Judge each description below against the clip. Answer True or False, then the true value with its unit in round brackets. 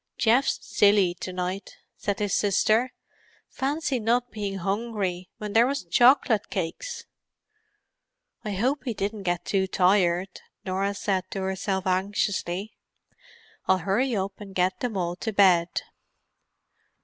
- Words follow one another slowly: True (130 wpm)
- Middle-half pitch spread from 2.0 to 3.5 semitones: True (3.0 semitones)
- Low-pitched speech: False (200 Hz)